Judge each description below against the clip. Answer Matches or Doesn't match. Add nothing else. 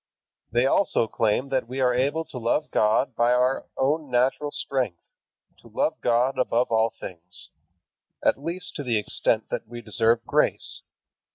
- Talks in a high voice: Doesn't match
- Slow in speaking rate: Doesn't match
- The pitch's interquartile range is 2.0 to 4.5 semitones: Matches